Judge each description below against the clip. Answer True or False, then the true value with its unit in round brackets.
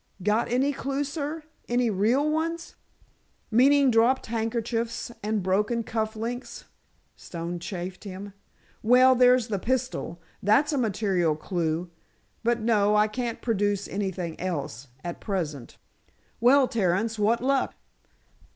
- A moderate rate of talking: False (120 wpm)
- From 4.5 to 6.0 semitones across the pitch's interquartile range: True (4.8 semitones)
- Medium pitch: False (220 Hz)